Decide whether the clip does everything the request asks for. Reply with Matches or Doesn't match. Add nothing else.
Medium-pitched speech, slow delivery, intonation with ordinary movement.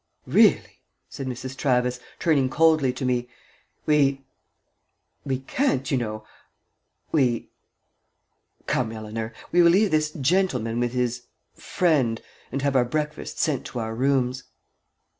Doesn't match